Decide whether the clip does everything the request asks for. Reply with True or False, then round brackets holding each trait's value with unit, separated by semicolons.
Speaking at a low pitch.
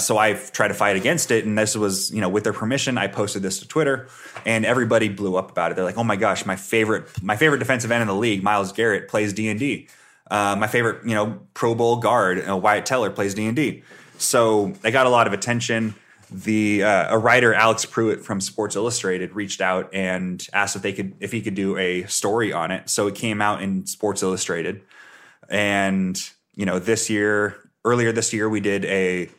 True (105 Hz)